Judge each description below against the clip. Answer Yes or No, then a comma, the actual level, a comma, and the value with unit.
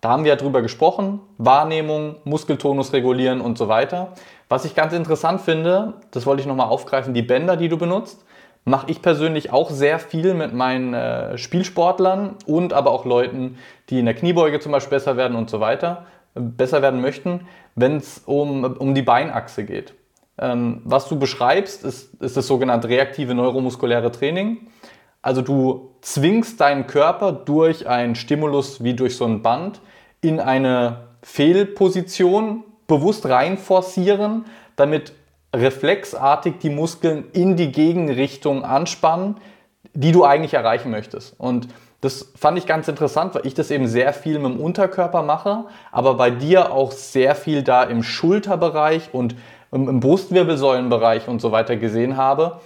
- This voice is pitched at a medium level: Yes, medium, 145 Hz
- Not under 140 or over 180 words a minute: Yes, average, 155 wpm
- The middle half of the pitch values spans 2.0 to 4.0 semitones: No, average, 5.3 semitones